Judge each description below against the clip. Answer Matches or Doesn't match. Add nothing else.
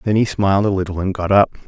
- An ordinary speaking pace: Doesn't match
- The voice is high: Doesn't match